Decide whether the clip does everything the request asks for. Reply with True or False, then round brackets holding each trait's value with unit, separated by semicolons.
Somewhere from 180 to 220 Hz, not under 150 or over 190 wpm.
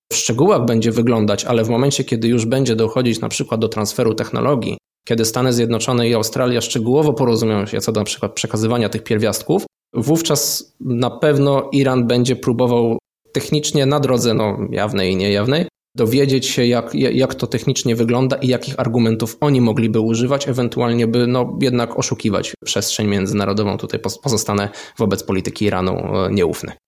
False (120 Hz; 155 wpm)